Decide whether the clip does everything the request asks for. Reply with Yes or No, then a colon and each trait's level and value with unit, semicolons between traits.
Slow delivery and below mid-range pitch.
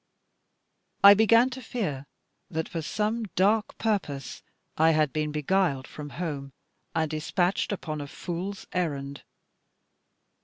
No: slow, 120 wpm; medium, 165 Hz